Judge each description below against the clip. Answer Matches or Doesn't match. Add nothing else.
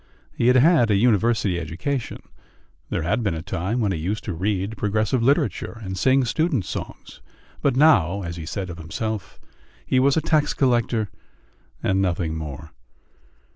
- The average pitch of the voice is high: Doesn't match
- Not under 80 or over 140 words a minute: Doesn't match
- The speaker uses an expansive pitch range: Matches